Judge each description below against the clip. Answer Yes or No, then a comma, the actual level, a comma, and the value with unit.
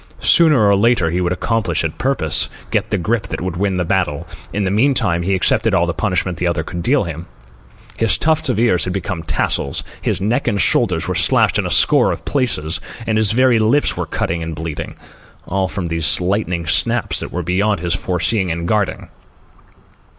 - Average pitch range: Yes, average, 4.4 semitones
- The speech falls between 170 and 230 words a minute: Yes, average, 195 wpm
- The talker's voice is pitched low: Yes, very low, 95 Hz